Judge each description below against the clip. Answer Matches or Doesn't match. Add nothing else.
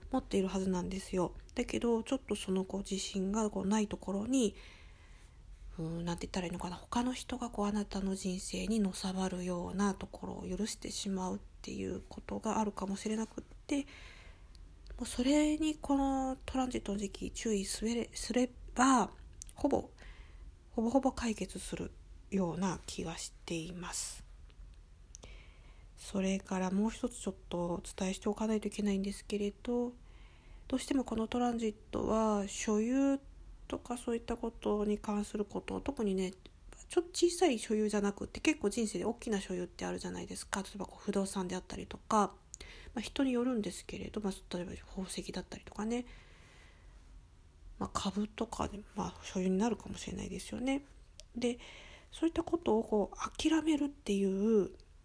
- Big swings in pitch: Doesn't match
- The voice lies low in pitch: Doesn't match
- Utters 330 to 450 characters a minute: Matches